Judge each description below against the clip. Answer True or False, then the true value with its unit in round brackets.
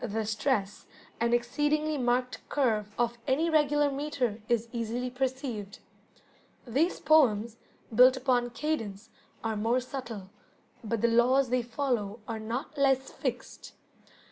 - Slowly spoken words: True (125 wpm)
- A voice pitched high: True (245 Hz)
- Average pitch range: True (3.3 semitones)